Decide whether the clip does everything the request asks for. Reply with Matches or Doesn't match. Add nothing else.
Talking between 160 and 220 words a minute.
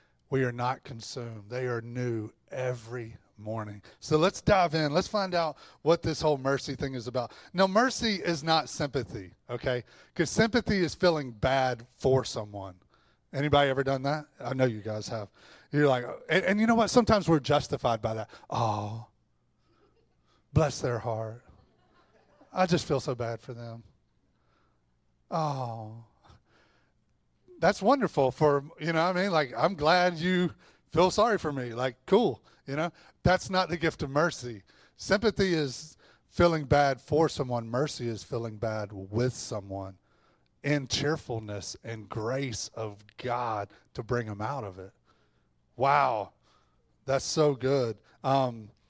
Doesn't match